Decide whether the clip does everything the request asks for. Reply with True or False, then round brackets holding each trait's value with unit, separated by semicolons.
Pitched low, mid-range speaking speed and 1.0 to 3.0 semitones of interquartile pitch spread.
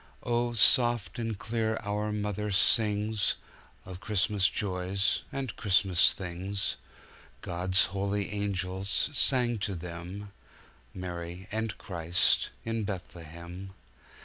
False (100 Hz; 90 wpm; 2.7 semitones)